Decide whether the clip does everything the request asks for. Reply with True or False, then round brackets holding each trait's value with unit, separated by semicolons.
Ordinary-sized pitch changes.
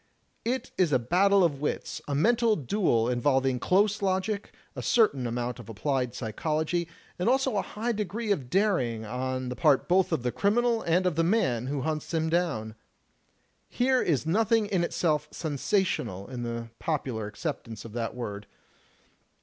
False (8.3 semitones)